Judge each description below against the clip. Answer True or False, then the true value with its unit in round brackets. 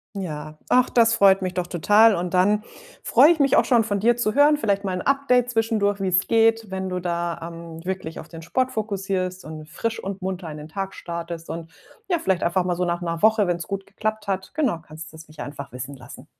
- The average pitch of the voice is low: False (190 Hz)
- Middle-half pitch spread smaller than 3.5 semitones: False (4.4 semitones)